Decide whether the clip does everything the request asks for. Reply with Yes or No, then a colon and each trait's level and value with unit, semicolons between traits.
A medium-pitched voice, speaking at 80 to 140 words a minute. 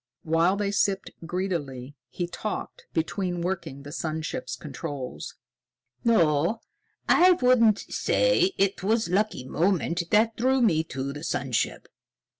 Yes: medium, 180 Hz; slow, 135 wpm